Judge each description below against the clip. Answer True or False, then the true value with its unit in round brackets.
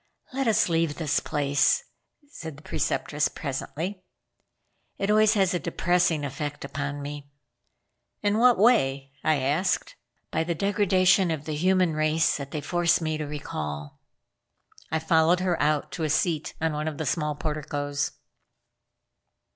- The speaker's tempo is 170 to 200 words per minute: False (145 wpm)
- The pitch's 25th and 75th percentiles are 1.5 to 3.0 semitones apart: False (3.6 semitones)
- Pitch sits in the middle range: True (155 Hz)